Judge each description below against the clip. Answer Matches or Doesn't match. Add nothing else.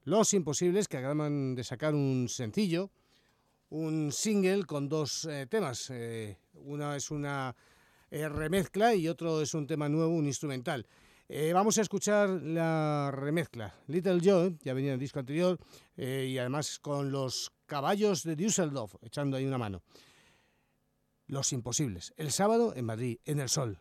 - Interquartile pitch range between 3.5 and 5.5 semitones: Matches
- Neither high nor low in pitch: Matches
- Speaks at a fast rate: Doesn't match